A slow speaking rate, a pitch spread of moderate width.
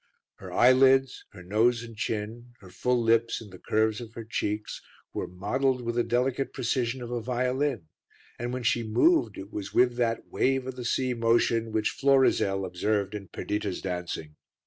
No: average, 175 wpm; average, 3.1 semitones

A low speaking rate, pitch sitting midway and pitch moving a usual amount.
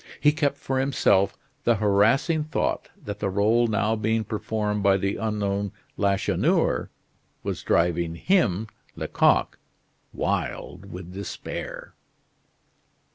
No: slow, 110 wpm; low, 105 Hz; average, 3.0 semitones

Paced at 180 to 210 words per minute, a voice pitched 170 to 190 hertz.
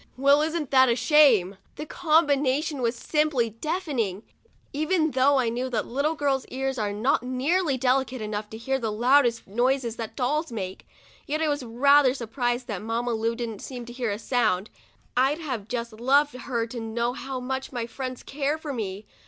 No: average, 185 wpm; very high, 255 Hz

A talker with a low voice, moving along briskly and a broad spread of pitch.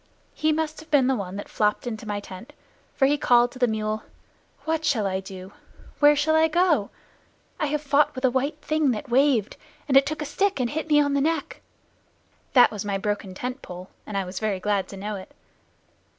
No: very high, 255 Hz; fast, 220 wpm; wide, 6.3 semitones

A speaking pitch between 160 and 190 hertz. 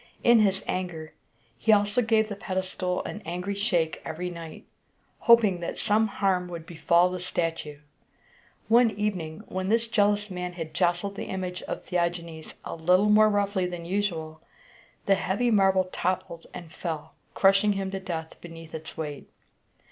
Yes: medium, 185 Hz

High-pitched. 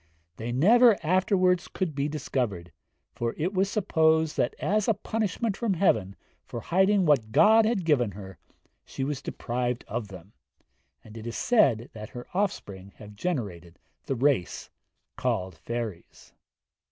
No: low, 135 Hz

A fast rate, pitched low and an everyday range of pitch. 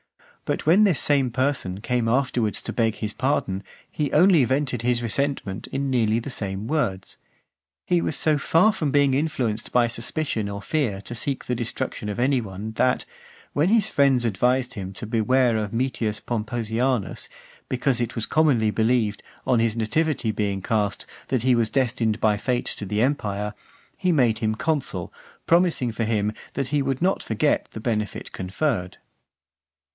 No: average, 170 wpm; low, 120 Hz; average, 4.3 semitones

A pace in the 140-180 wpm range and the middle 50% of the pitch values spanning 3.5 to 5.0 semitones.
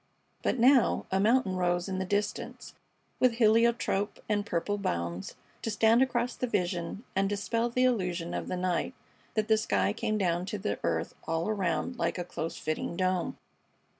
Yes: average, 170 wpm; average, 4.3 semitones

